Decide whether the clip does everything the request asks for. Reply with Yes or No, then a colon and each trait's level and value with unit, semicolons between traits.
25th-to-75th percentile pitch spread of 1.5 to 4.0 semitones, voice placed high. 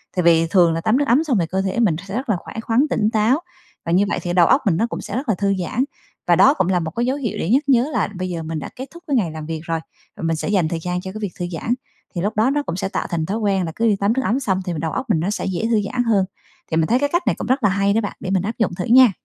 No: average, 5.2 semitones; high, 200 Hz